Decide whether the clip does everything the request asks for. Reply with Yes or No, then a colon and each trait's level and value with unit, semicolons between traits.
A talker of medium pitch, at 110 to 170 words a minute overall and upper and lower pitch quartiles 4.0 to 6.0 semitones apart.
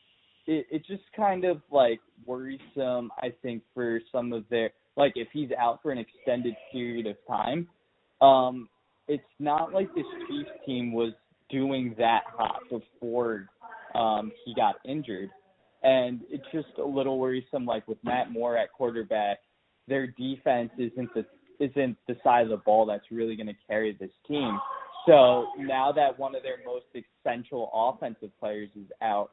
No: low, 125 Hz; average, 160 wpm; average, 4.3 semitones